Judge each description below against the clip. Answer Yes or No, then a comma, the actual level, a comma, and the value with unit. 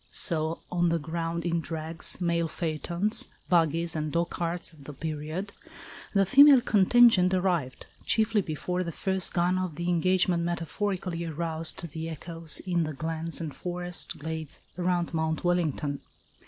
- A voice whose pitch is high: No, medium, 170 Hz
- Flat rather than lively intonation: Yes, narrow, 2.0 semitones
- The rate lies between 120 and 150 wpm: Yes, average, 140 wpm